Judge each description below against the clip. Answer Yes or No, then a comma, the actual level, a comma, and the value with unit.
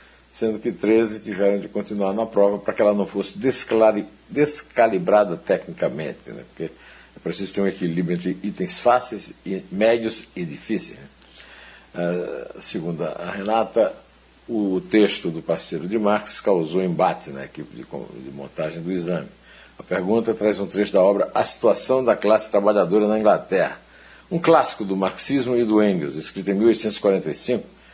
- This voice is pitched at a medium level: No, low, 105 Hz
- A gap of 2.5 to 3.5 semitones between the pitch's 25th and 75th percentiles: Yes, average, 3.0 semitones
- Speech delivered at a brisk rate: No, average, 155 wpm